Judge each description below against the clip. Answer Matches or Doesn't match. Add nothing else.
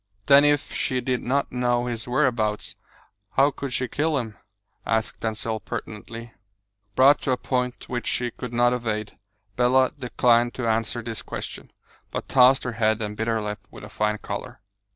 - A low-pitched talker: Matches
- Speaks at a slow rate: Doesn't match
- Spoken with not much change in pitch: Matches